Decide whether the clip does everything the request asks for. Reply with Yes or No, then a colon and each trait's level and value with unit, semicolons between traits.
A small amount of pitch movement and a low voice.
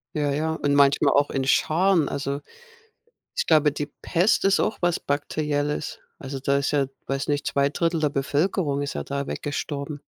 No: narrow, 1.8 semitones; medium, 145 Hz